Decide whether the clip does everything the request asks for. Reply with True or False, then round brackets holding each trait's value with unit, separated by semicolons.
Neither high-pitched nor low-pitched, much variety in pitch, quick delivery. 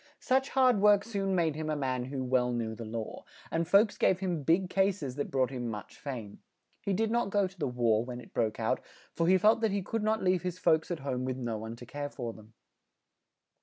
True (155 Hz; 7.8 semitones; 240 wpm)